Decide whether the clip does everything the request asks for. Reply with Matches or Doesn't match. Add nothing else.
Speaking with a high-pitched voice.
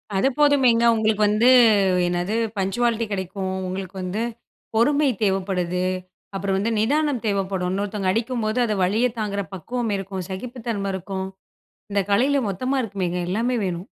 Matches